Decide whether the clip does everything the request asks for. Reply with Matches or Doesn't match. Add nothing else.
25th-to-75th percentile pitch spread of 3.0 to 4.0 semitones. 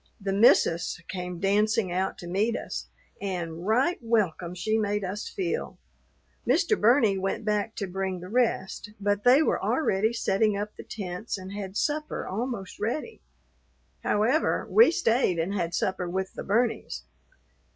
Matches